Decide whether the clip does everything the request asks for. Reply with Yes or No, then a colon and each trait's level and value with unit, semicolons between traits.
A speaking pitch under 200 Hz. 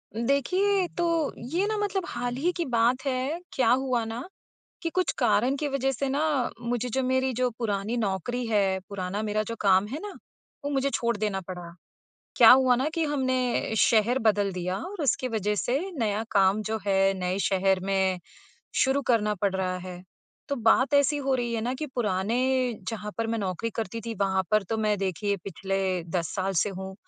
No: high, 230 Hz